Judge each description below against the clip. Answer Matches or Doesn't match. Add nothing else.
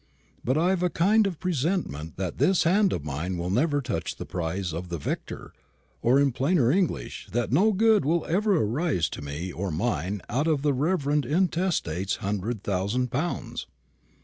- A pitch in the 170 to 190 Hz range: Doesn't match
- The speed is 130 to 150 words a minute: Doesn't match